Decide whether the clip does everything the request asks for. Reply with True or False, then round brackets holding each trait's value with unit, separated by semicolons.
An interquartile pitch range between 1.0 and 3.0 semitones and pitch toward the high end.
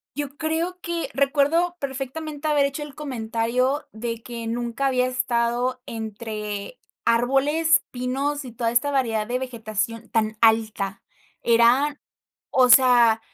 False (3.7 semitones; 250 Hz)